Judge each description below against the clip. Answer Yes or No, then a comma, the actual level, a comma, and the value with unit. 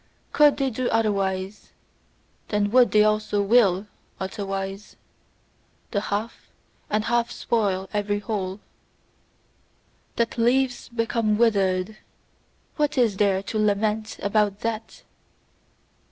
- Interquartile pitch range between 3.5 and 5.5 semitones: No, narrow, 2.4 semitones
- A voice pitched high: Yes, high, 215 Hz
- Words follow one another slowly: Yes, slow, 105 wpm